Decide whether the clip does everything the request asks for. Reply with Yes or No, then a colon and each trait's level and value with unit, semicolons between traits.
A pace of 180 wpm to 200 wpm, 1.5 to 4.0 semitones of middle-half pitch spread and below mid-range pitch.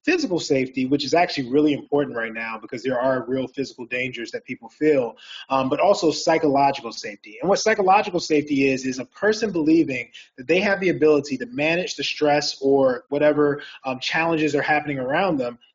No: average, 185 wpm; average, 3.5 semitones; medium, 145 Hz